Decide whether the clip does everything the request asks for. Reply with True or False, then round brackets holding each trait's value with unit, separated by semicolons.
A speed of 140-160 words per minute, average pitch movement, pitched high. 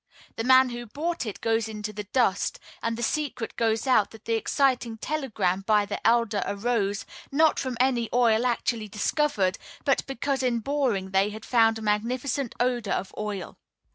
False (175 wpm; 3.4 semitones; 230 Hz)